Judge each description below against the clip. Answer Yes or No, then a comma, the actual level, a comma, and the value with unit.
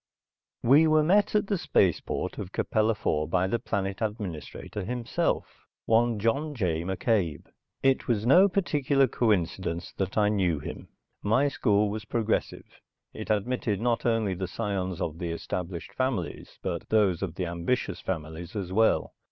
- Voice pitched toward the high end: No, low, 105 Hz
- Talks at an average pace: Yes, average, 155 wpm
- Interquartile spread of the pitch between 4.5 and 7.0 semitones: Yes, average, 4.8 semitones